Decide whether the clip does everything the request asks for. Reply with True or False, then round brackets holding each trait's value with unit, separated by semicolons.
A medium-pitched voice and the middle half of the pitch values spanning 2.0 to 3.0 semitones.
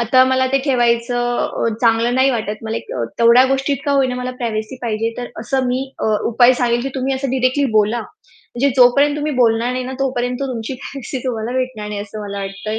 False (245 Hz; 2.6 semitones)